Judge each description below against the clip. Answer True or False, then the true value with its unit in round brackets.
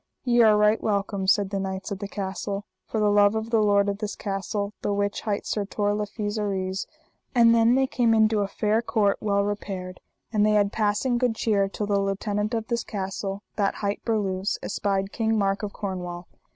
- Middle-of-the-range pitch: False (205 Hz)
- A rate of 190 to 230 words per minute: True (205 wpm)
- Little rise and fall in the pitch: True (1.7 semitones)